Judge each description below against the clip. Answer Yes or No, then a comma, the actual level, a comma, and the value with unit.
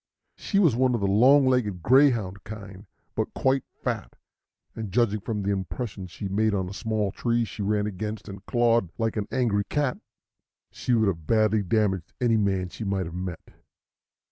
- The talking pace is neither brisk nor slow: Yes, average, 180 wpm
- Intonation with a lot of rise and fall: No, average, 3.2 semitones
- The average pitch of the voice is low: Yes, low, 105 Hz